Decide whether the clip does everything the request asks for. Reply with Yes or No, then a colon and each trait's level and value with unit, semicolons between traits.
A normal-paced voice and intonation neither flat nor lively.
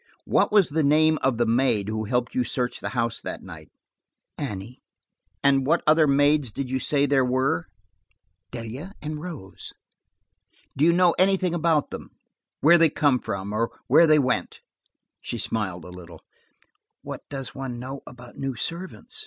Yes: average, 160 wpm; average, 4.6 semitones